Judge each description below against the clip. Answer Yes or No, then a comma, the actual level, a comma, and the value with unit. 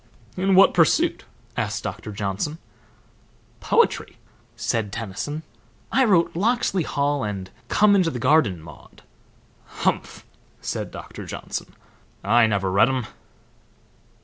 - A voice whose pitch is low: Yes, low, 130 Hz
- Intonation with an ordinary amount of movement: No, wide, 9.0 semitones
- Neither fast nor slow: No, slow, 115 wpm